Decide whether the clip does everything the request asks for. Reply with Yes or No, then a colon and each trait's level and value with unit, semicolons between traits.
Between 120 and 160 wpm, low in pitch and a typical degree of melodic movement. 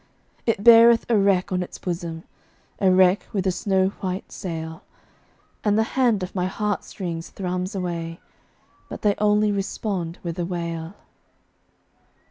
No: average, 145 wpm; medium, 185 Hz; average, 3.0 semitones